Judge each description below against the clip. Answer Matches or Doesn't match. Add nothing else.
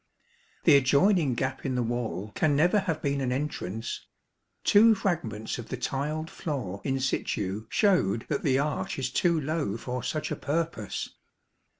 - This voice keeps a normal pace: Matches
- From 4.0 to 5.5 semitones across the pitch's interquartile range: Matches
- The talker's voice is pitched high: Doesn't match